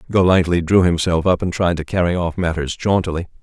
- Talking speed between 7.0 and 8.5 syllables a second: No, 5.8 syllables/s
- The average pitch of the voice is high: No, very low, 85 Hz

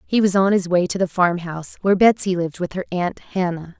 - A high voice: No, medium, 180 Hz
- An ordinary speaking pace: No, fast, 235 wpm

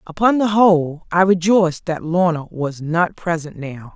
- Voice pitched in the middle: Yes, medium, 170 Hz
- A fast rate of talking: No, average, 165 wpm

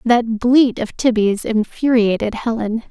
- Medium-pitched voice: No, high, 230 Hz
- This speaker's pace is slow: Yes, slow, 125 wpm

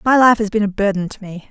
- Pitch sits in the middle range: No, high, 210 Hz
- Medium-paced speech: No, fast, 320 wpm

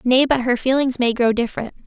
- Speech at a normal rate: No, fast, 225 wpm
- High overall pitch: Yes, very high, 250 Hz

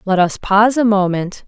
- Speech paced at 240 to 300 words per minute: No, fast, 205 wpm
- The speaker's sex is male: No, female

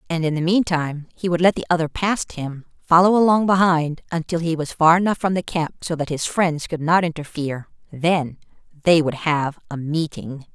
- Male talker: No, female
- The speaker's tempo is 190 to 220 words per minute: Yes, average, 195 wpm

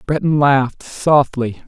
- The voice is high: No, medium, 140 Hz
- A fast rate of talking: No, slow, 105 wpm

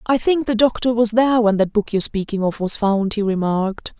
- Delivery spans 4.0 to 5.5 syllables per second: No, 5.7 syllables/s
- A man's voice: No, female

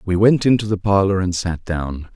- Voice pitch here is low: Yes, very low, 95 Hz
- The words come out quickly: Yes, fast, 220 wpm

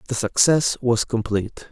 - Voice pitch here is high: No, low, 115 Hz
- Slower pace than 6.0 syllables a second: Yes, 4.8 syllables/s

